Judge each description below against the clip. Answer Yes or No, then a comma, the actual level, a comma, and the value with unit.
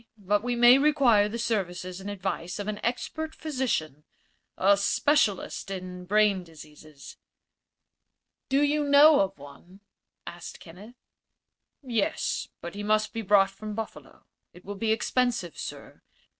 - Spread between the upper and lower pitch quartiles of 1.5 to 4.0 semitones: No, average, 4.7 semitones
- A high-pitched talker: Yes, high, 205 Hz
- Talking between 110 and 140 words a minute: Yes, slow, 135 wpm